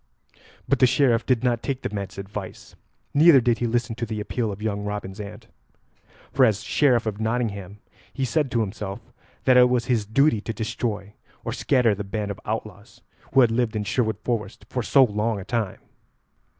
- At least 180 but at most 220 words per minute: Yes, average, 190 wpm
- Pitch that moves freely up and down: No, average, 3.2 semitones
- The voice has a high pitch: No, low, 110 Hz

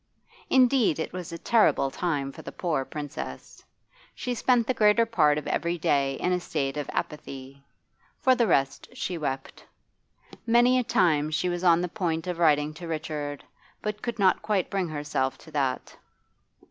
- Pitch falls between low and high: Yes, medium, 165 Hz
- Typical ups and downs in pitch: No, wide, 6.1 semitones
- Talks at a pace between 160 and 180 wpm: Yes, average, 170 wpm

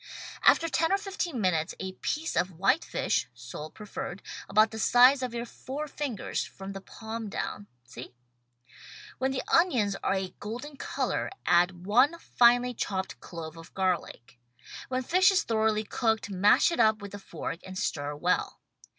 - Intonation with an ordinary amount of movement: No, wide, 5.8 semitones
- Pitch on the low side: No, high, 215 Hz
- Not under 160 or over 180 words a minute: Yes, average, 170 wpm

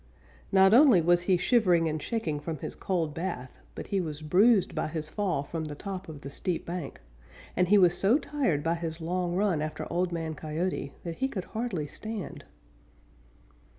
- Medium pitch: Yes, medium, 175 Hz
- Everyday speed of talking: Yes, average, 185 wpm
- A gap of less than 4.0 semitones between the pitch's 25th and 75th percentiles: Yes, average, 3.6 semitones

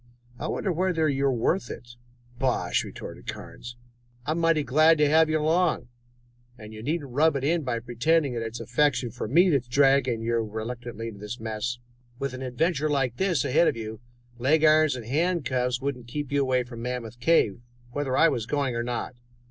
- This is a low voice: Yes, low, 130 Hz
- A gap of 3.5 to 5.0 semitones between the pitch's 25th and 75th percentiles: Yes, average, 4.5 semitones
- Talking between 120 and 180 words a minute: No, average, 195 wpm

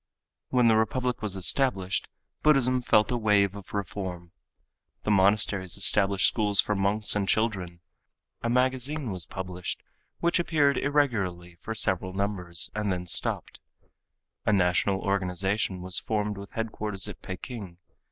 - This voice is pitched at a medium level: No, low, 100 Hz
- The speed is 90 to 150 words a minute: Yes, slow, 135 wpm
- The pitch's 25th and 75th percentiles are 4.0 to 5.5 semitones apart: No, average, 3.4 semitones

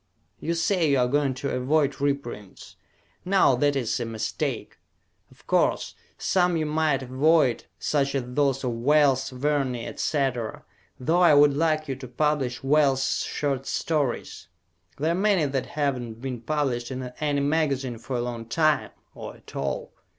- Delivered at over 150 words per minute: Yes, average, 160 wpm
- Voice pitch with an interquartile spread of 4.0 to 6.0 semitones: No, average, 3.2 semitones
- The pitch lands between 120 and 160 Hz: Yes, medium, 140 Hz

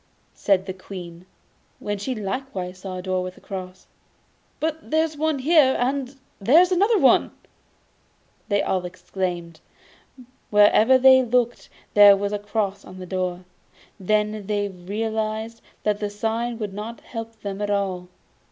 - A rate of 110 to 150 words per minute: Yes, average, 145 wpm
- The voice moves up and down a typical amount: Yes, average, 4.1 semitones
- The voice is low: No, high, 205 Hz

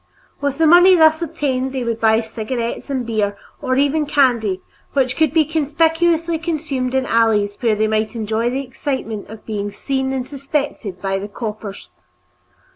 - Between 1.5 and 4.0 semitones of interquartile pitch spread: No, average, 5.2 semitones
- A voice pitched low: No, very high, 255 Hz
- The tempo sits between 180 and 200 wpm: No, average, 170 wpm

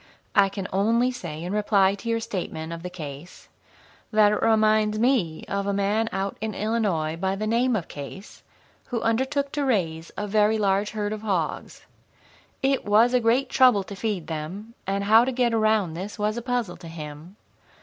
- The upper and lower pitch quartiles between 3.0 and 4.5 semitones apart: Yes, average, 3.5 semitones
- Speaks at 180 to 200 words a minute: Yes, average, 190 wpm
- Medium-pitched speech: No, high, 210 Hz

